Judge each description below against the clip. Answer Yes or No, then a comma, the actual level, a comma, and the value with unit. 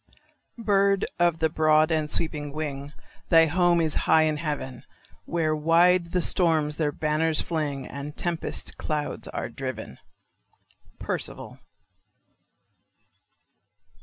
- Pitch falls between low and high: Yes, medium, 155 Hz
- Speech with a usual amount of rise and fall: No, narrow, 2.1 semitones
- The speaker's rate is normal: No, slow, 115 wpm